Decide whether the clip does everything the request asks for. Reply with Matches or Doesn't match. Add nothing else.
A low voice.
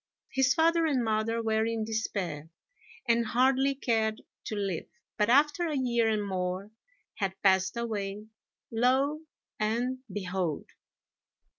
Doesn't match